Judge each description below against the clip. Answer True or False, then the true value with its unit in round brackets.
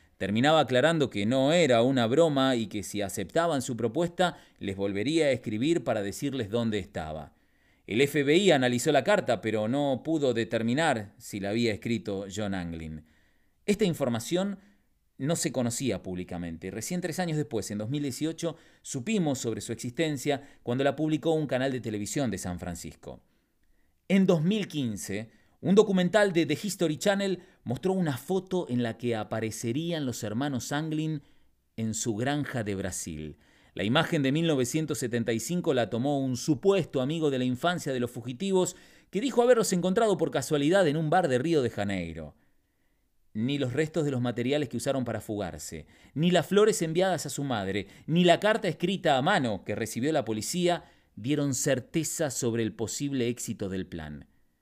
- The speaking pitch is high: False (135 Hz)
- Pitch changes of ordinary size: False (6.9 semitones)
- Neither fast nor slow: True (165 wpm)